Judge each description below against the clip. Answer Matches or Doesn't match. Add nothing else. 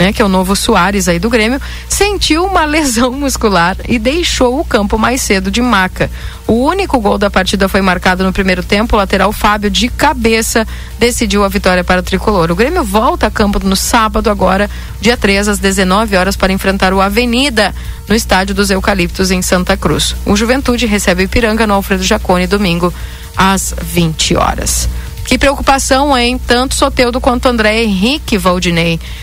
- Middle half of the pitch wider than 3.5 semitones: Matches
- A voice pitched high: Matches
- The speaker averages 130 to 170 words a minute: Doesn't match